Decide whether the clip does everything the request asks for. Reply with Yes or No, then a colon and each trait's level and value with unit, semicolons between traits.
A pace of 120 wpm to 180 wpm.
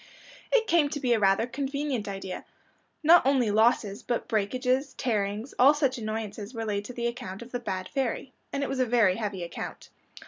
No: average, 195 wpm